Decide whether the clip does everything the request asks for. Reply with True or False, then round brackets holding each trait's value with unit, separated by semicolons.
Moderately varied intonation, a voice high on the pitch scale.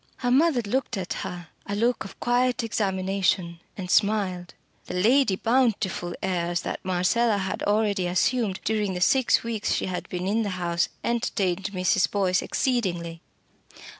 True (4.1 semitones; 195 Hz)